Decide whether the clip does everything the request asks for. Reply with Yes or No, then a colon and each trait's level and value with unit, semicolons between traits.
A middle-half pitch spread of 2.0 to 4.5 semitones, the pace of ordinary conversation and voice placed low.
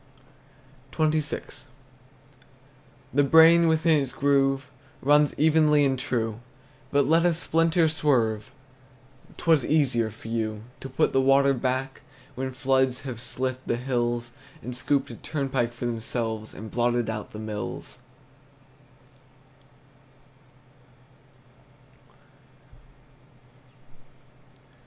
No: average, 3.6 semitones; slow, 100 wpm; low, 130 Hz